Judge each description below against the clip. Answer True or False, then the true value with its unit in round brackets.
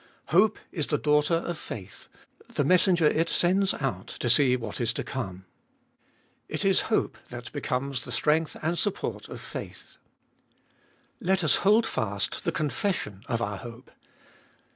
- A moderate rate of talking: True (150 wpm)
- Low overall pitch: False (145 Hz)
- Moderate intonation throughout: False (6.6 semitones)